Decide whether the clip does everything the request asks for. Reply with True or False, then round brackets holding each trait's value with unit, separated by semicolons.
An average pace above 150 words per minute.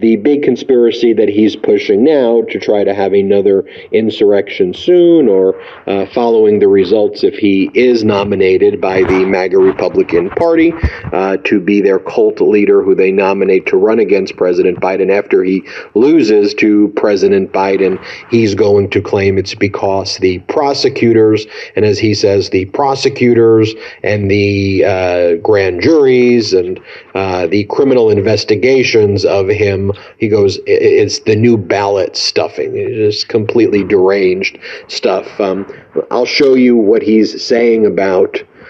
False (145 wpm)